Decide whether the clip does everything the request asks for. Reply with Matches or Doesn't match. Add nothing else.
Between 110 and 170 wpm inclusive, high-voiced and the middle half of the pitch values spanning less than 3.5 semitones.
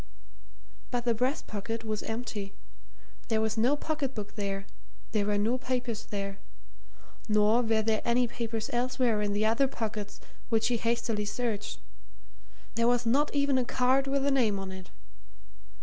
Matches